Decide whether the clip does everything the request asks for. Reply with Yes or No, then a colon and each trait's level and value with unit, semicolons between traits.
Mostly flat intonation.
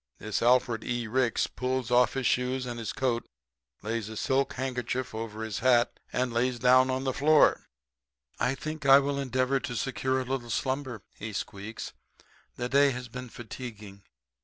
Yes: narrow, 2.1 semitones